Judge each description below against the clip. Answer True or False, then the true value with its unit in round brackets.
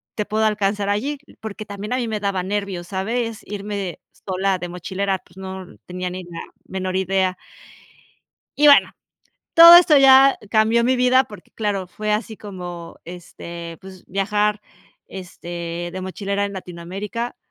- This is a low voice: False (200 Hz)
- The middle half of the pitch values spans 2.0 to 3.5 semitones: True (2.8 semitones)